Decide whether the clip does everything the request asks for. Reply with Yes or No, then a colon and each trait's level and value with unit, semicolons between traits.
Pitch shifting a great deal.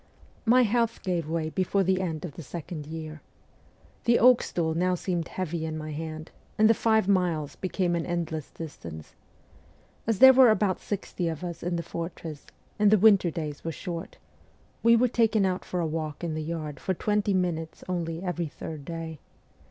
No: average, 3.6 semitones